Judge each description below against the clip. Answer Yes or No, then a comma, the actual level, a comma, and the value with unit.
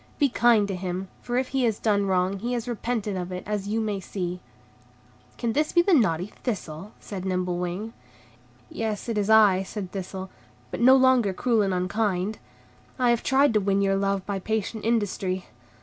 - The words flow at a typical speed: Yes, average, 185 wpm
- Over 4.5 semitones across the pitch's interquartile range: No, average, 3.5 semitones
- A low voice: No, high, 205 Hz